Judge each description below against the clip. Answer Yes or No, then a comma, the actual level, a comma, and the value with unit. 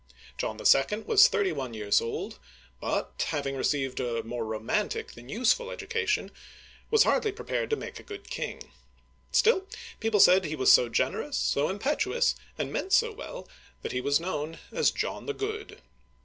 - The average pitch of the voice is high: Yes, high, 210 Hz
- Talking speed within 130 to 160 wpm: No, average, 170 wpm